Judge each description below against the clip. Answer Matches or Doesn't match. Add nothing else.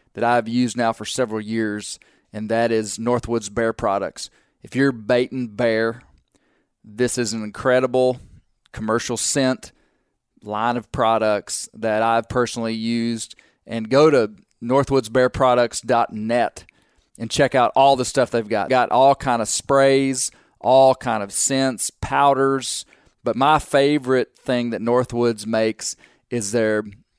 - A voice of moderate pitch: Doesn't match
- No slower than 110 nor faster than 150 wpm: Matches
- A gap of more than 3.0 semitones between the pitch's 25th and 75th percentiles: Doesn't match